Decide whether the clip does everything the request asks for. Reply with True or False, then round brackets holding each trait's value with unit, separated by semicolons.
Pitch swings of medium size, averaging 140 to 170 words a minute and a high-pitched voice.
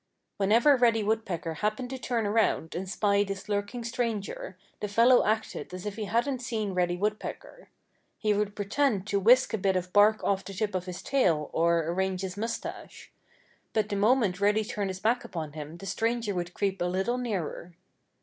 False (3.4 semitones; 190 wpm; 205 Hz)